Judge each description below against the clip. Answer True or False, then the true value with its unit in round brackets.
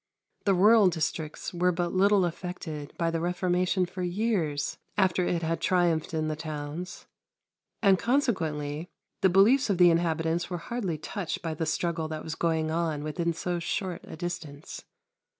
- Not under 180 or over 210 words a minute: False (160 wpm)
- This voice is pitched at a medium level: True (170 Hz)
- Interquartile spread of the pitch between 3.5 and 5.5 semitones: False (2.5 semitones)